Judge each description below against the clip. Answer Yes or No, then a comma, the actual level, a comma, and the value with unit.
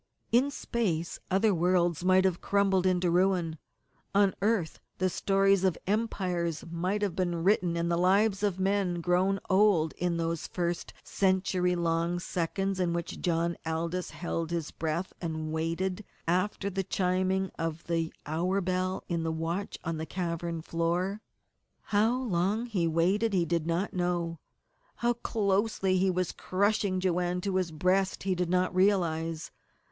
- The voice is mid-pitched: Yes, medium, 180 Hz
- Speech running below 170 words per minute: Yes, average, 150 wpm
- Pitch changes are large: No, narrow, 2.4 semitones